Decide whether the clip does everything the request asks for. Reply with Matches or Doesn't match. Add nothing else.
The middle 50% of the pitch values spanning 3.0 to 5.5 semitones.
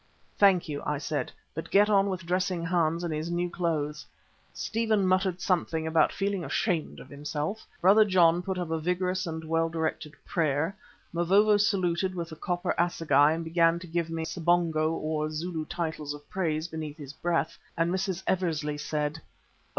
Doesn't match